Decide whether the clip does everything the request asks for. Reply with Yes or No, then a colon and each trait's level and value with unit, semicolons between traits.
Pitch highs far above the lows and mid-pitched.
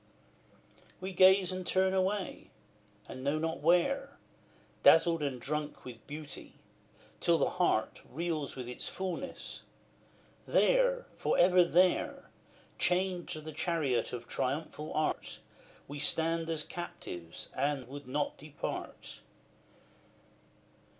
No: average, 4.2 semitones; medium, 160 Hz